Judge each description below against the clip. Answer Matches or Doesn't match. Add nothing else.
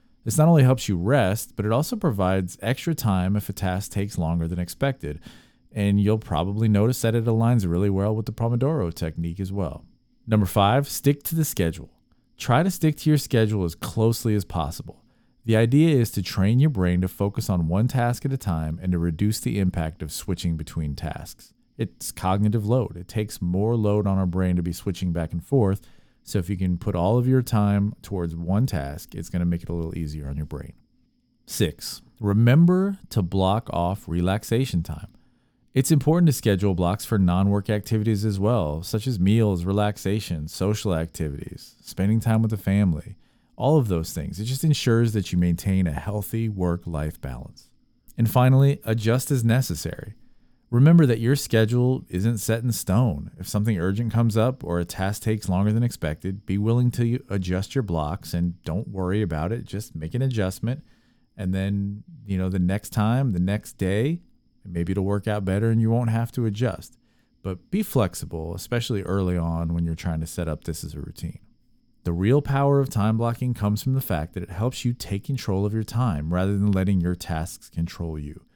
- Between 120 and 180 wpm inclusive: Doesn't match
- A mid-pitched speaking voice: Doesn't match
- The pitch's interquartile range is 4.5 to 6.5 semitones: Matches